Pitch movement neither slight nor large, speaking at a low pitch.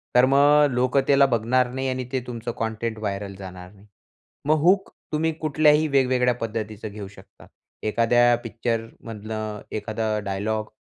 Yes: average, 3.6 semitones; low, 115 Hz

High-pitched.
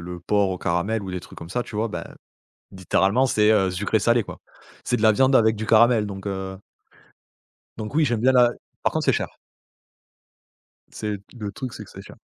No: low, 105 Hz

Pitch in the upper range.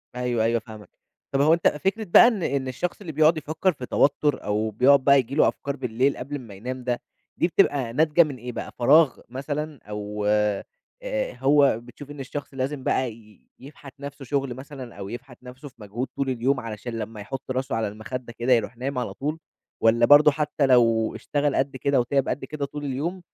No: low, 130 Hz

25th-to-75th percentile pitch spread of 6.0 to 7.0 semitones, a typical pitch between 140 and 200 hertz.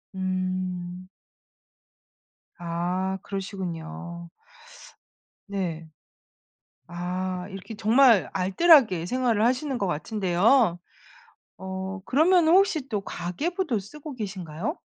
No: wide, 5.4 semitones; high, 190 Hz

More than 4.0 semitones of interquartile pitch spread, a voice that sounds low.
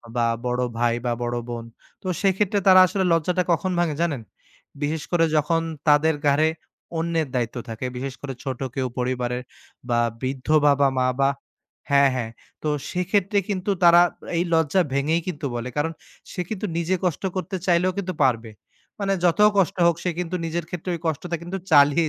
No: average, 5.1 semitones; medium, 160 Hz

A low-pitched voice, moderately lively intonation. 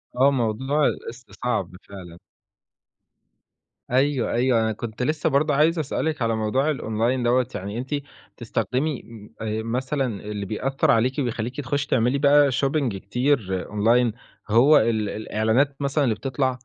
Yes: low, 125 Hz; average, 3.9 semitones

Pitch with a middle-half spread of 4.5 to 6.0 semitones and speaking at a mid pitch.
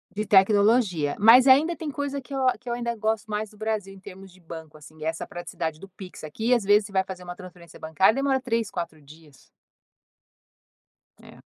No: average, 5.3 semitones; high, 200 Hz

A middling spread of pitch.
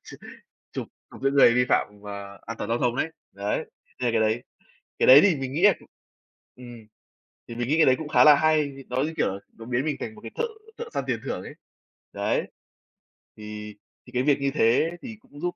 Yes: average, 5.0 semitones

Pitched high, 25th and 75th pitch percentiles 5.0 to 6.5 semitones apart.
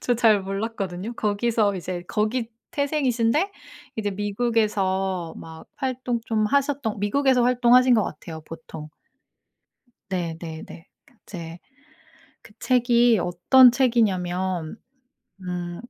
Yes: high, 215 Hz; average, 5.3 semitones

